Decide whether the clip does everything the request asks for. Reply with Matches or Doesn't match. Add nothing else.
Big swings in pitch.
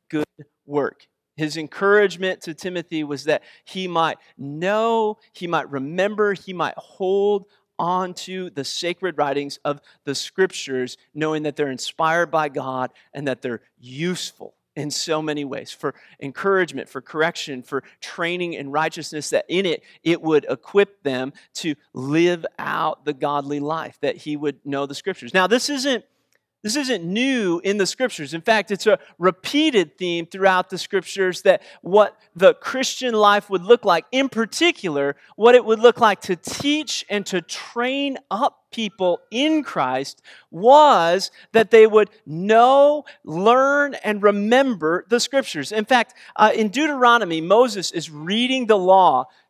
Matches